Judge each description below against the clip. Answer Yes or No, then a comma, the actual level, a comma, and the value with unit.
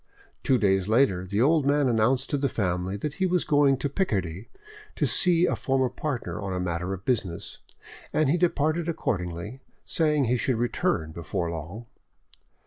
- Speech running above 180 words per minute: No, average, 170 wpm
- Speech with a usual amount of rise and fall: No, wide, 7.5 semitones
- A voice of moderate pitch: No, low, 120 Hz